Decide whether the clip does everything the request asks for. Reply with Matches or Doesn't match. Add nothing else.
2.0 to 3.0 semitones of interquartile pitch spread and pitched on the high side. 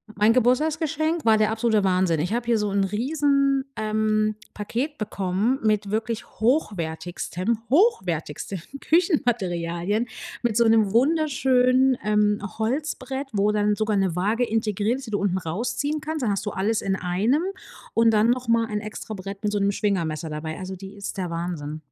Doesn't match